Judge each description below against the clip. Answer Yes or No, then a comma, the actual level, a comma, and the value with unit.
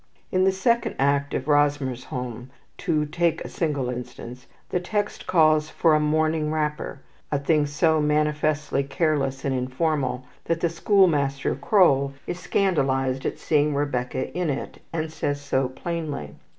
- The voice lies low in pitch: No, medium, 150 Hz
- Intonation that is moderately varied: Yes, average, 3.1 semitones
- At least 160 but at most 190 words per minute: No, average, 150 wpm